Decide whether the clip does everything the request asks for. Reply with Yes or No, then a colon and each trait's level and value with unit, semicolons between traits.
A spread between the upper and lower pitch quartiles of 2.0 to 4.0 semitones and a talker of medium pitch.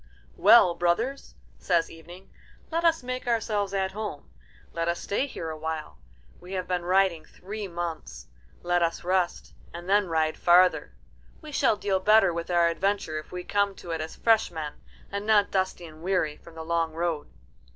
Yes: average, 3.3 semitones; medium, 180 Hz